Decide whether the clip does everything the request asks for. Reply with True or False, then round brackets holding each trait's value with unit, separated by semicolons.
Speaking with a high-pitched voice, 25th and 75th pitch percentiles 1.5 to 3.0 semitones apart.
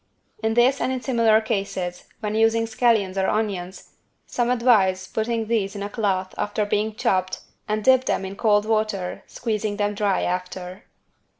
True (210 Hz; 2.7 semitones)